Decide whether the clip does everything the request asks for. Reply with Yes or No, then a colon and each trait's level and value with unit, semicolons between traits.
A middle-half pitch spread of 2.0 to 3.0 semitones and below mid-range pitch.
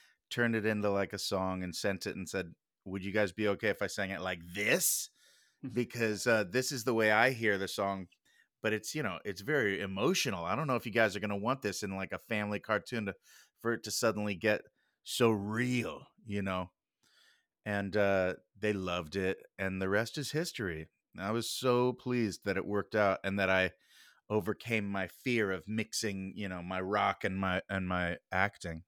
Yes: average, 2.7 semitones; low, 100 Hz